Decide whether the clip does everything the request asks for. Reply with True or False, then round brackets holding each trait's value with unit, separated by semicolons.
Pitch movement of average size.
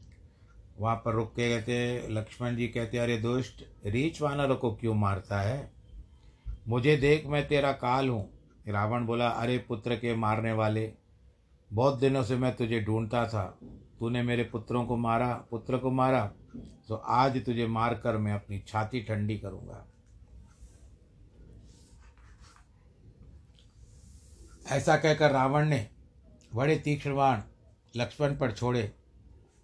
True (3.2 semitones)